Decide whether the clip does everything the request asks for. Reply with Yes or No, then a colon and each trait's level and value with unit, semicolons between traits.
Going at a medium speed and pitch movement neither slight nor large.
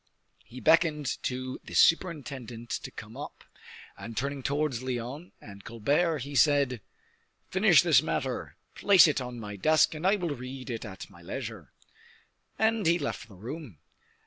Yes: average, 155 wpm; average, 4.8 semitones